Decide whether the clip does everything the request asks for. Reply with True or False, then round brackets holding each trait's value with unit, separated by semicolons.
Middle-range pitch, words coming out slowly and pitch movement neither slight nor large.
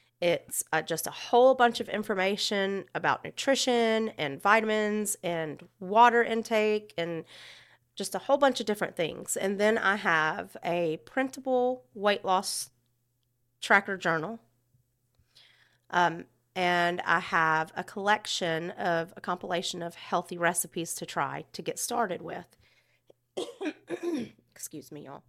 True (180 Hz; 130 wpm; 4.9 semitones)